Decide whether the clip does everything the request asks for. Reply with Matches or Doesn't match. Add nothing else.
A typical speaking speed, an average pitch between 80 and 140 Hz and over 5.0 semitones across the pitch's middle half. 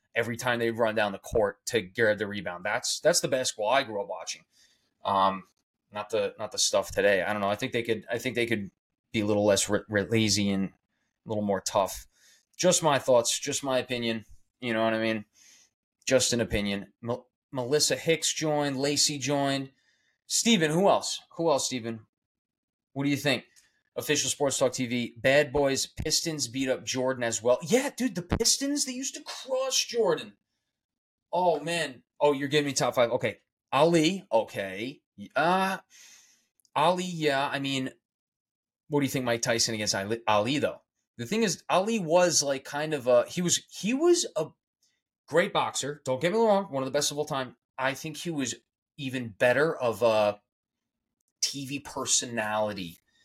Matches